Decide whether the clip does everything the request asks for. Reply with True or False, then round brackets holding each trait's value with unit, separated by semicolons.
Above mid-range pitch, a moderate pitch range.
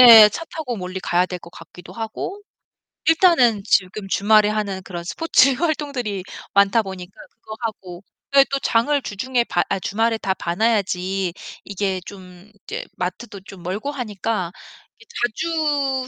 True (210 Hz; 5.0 semitones)